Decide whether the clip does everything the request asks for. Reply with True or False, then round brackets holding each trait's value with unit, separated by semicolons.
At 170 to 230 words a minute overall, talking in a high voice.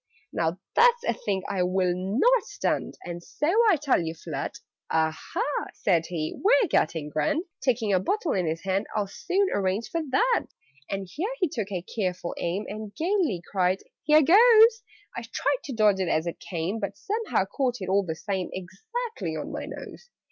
True (185 wpm; 200 Hz)